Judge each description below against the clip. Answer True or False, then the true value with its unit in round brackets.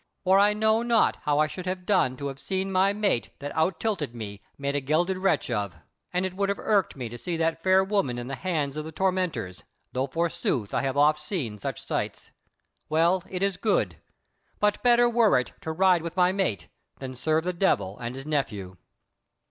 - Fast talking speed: True (210 wpm)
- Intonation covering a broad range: True (6.1 semitones)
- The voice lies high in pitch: False (165 Hz)